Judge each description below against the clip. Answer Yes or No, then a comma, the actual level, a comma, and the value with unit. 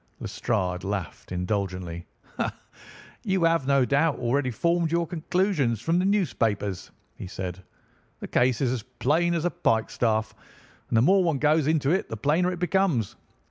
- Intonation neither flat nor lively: No, wide, 7.7 semitones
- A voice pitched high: No, medium, 140 Hz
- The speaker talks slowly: No, average, 155 wpm